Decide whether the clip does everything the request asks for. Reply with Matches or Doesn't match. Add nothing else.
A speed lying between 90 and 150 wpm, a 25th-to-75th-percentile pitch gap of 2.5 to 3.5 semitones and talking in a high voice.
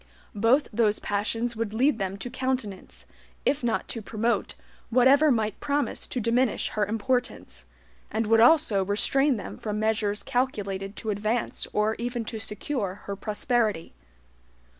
Matches